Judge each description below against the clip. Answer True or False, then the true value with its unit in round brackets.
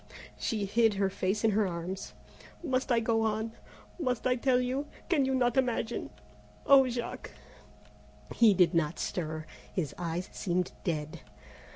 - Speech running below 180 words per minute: True (155 wpm)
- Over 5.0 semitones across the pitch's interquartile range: True (5.6 semitones)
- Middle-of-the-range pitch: False (220 Hz)